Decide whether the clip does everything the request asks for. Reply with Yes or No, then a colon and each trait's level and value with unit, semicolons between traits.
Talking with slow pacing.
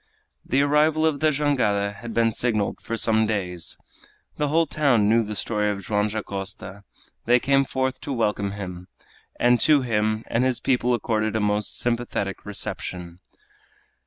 No: average, 160 wpm